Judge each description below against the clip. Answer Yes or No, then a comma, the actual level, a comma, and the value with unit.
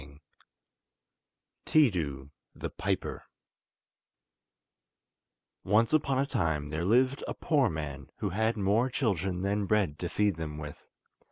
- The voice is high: No, low, 100 Hz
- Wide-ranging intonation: Yes, wide, 7.0 semitones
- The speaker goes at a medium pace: No, slow, 120 wpm